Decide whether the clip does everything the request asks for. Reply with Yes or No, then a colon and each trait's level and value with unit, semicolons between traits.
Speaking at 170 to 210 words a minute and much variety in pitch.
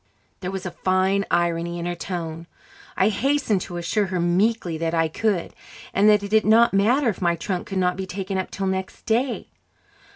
No: average, 200 wpm; average, 3.3 semitones